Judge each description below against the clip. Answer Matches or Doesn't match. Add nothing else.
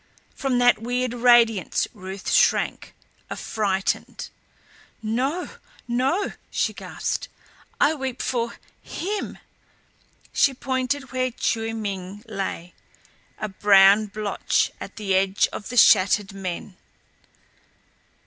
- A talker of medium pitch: Doesn't match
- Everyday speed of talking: Doesn't match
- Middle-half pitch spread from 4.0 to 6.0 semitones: Matches